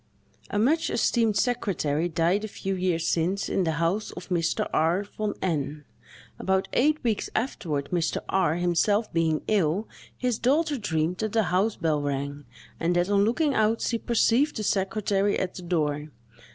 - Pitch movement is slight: No, average, 4.8 semitones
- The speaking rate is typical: Yes, average, 165 wpm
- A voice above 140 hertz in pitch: Yes, high, 190 Hz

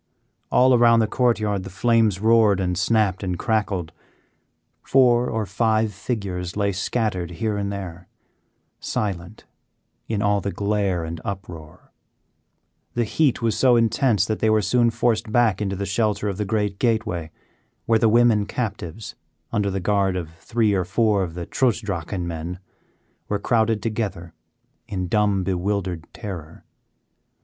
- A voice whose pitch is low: Yes, low, 105 Hz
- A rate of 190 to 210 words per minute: No, average, 150 wpm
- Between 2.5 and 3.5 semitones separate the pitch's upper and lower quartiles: Yes, average, 3.2 semitones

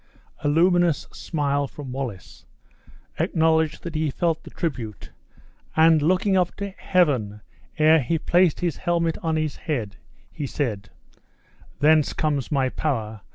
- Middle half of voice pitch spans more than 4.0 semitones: No, average, 3.6 semitones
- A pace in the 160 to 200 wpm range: No, slow, 135 wpm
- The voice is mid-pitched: Yes, medium, 155 Hz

